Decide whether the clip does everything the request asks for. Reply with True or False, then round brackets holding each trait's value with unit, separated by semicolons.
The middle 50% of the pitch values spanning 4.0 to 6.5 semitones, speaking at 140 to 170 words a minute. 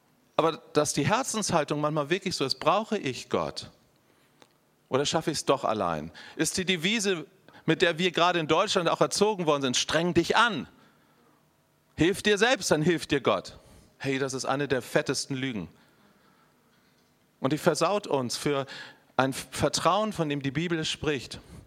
True (4.3 semitones; 165 wpm)